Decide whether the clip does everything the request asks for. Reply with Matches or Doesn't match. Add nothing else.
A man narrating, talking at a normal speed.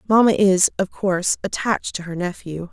Doesn't match